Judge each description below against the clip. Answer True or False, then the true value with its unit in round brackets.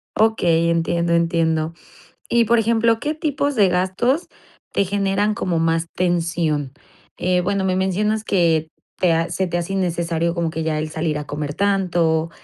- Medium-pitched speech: True (175 Hz)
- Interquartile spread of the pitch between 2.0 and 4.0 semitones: True (3.5 semitones)